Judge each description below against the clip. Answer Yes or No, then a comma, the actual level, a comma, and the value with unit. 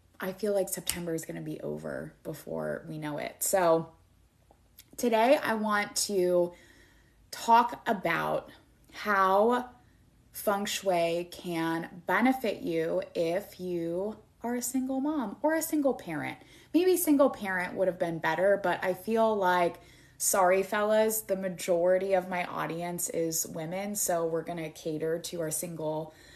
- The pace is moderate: Yes, average, 145 wpm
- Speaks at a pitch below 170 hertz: No, medium, 185 Hz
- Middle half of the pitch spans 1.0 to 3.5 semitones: No, average, 4.2 semitones